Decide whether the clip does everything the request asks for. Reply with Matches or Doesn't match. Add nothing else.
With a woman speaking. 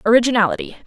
Matches